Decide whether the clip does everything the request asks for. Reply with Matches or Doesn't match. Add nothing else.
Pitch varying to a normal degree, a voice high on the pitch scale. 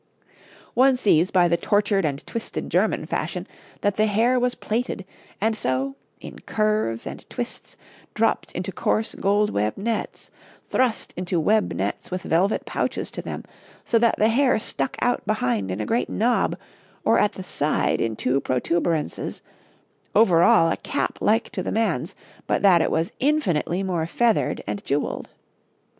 Doesn't match